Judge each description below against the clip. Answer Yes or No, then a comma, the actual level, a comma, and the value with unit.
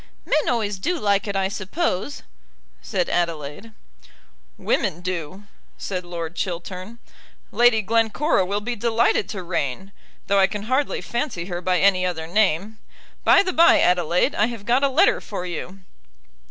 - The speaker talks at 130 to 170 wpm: Yes, average, 155 wpm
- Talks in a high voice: Yes, high, 200 Hz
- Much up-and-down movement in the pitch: No, average, 4.4 semitones